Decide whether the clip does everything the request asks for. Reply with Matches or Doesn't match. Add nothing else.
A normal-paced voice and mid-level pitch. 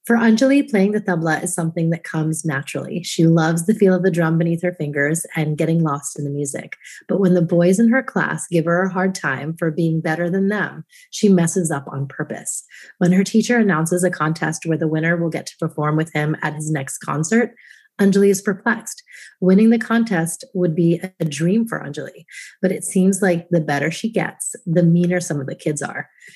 Doesn't match